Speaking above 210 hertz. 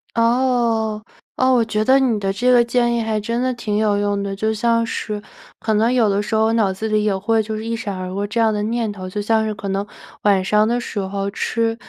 Yes: high, 220 Hz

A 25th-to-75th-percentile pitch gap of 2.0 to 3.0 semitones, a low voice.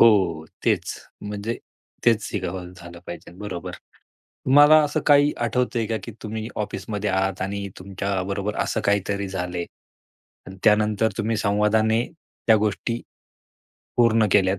Yes: average, 2.7 semitones; low, 105 Hz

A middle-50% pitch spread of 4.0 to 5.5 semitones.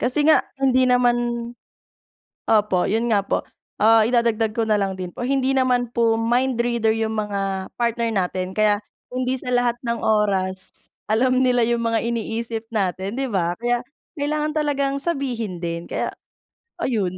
No: average, 3.1 semitones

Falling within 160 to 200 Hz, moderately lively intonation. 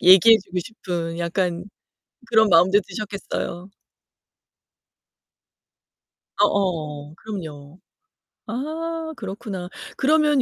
Yes: high, 190 Hz; average, 4.6 semitones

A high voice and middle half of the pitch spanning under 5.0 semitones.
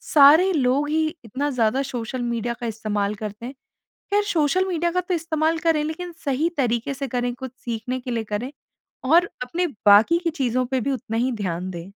No: very high, 260 Hz; wide, 5.6 semitones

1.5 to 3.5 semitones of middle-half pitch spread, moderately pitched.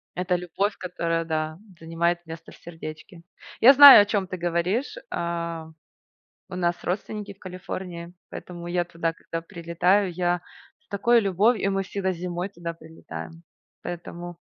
Yes: narrow, 2.5 semitones; medium, 175 Hz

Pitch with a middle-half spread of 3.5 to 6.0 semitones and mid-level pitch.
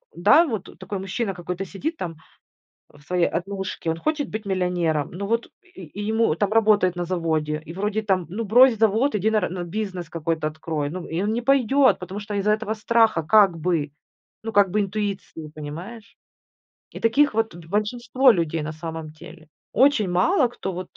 No: average, 4.5 semitones; high, 195 Hz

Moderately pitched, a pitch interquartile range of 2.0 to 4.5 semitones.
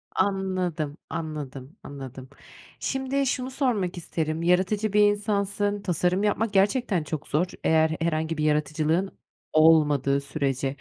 No: medium, 170 Hz; average, 4.9 semitones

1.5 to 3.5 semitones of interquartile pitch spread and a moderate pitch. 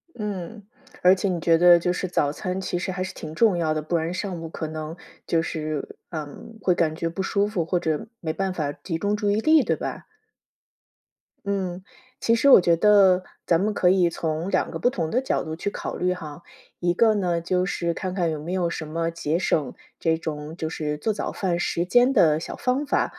Yes: average, 3.2 semitones; medium, 175 Hz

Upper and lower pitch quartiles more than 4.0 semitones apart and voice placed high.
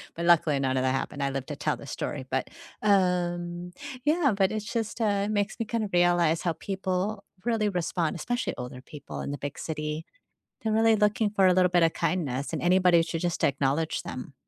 No: average, 5.1 semitones; medium, 175 Hz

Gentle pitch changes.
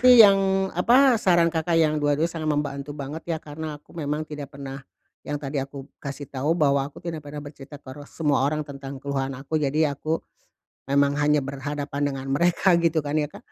Yes: narrow, 2.3 semitones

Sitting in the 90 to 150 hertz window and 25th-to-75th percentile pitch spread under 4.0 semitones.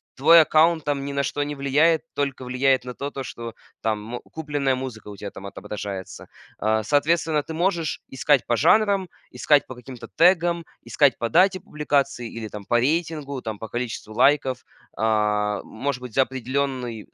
No: low, 135 Hz; average, 4.6 semitones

